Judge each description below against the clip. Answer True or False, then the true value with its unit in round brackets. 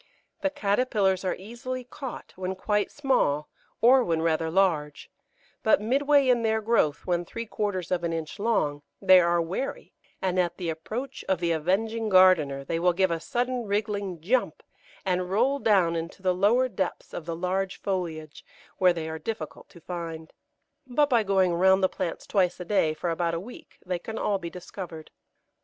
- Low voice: False (185 Hz)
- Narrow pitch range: False (4.6 semitones)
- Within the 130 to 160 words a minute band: False (180 wpm)